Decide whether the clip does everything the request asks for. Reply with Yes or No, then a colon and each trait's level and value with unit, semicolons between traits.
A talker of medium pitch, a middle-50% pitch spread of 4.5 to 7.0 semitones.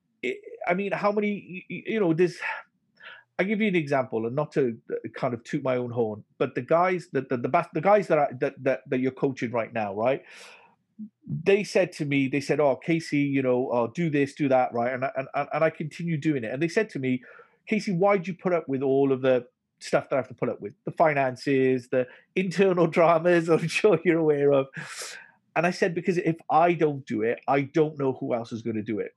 Yes: medium, 155 Hz; average, 5.1 semitones